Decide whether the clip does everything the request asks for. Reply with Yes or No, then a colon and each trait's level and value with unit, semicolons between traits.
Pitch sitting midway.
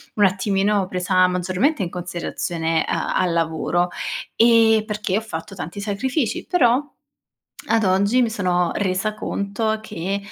No: high, 200 Hz